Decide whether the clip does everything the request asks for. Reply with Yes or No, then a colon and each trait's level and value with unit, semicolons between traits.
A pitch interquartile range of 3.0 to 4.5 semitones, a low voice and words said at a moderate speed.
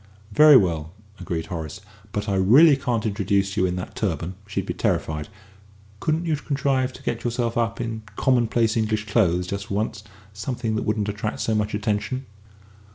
Yes: average, 3.5 semitones; low, 105 Hz; average, 170 wpm